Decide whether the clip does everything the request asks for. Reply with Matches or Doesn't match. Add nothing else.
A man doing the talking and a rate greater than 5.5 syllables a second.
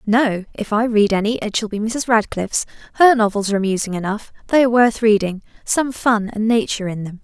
Doesn't match